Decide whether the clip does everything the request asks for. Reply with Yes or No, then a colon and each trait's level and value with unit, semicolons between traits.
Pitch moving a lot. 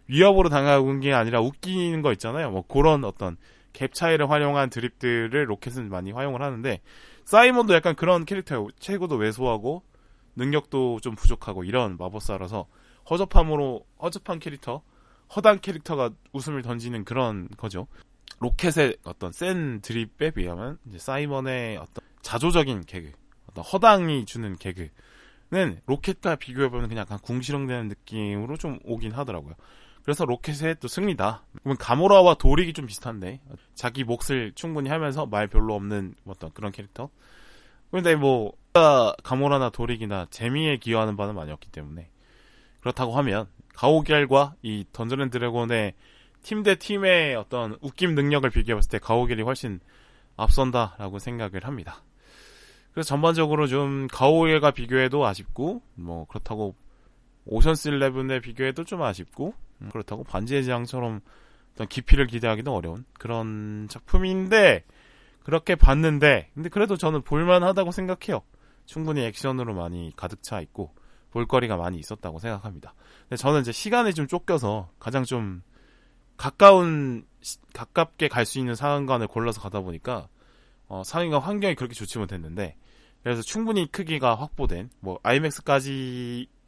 Yes: wide, 5.7 semitones